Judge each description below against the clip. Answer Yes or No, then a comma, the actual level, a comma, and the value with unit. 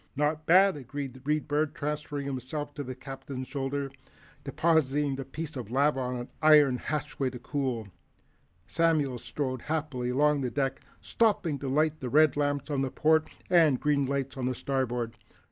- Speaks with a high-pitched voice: No, medium, 140 Hz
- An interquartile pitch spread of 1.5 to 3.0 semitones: Yes, narrow, 2.6 semitones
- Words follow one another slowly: No, average, 175 wpm